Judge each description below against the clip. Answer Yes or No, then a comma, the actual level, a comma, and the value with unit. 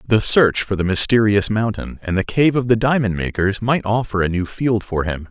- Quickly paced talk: Yes, fast, 225 wpm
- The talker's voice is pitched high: No, low, 105 Hz